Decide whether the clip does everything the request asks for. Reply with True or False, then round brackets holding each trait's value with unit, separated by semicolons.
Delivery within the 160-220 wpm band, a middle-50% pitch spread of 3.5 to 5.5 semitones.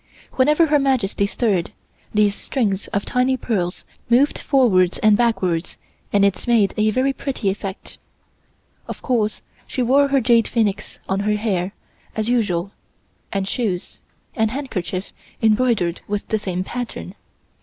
False (140 wpm; 4.2 semitones)